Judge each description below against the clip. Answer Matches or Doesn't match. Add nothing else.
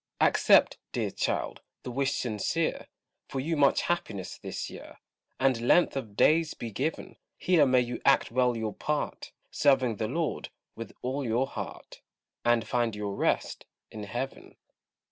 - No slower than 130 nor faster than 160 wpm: Matches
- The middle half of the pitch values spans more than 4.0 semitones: Doesn't match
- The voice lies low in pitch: Matches